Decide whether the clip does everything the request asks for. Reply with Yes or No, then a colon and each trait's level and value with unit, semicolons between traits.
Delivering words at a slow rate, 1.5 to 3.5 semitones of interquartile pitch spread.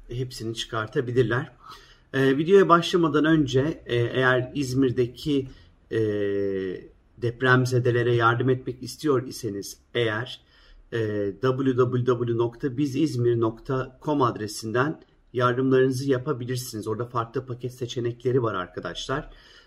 Yes: slow, 80 wpm; narrow, 2.5 semitones